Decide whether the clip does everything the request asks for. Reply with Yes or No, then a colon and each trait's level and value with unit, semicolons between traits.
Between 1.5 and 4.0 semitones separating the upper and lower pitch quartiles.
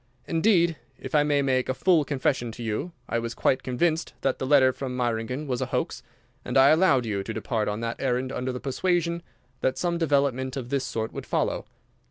Yes: average, 3.5 semitones